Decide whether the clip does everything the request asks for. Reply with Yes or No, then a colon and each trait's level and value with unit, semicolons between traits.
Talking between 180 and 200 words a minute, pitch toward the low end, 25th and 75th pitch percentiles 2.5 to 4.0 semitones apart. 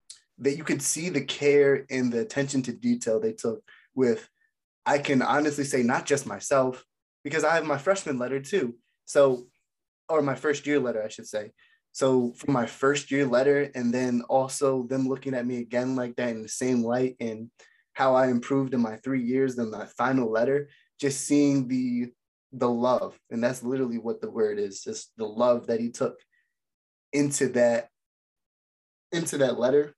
Yes: average, 185 wpm; low, 130 Hz; average, 2.8 semitones